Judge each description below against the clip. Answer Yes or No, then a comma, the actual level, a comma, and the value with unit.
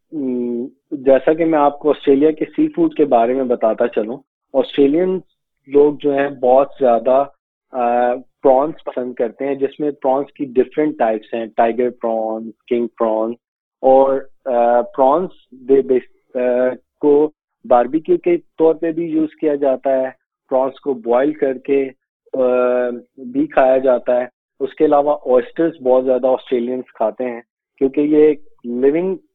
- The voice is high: No, low, 135 Hz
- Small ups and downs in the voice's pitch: No, average, 3.7 semitones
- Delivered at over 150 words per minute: No, average, 140 wpm